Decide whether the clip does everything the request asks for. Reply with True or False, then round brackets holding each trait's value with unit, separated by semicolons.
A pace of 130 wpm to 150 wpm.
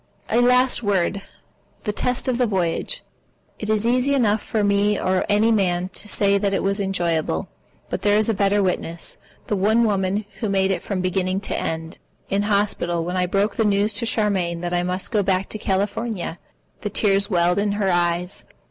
False (195 wpm)